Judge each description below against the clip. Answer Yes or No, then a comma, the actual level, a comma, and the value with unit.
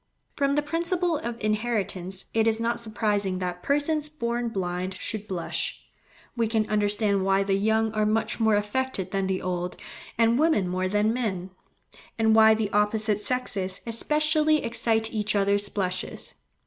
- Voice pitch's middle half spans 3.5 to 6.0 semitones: No, average, 3.1 semitones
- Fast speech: No, average, 155 wpm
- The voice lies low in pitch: No, high, 215 Hz